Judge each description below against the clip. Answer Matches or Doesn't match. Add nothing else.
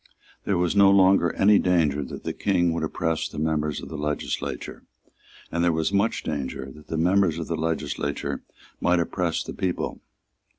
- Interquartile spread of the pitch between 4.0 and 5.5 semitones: Doesn't match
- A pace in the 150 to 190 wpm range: Matches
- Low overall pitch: Matches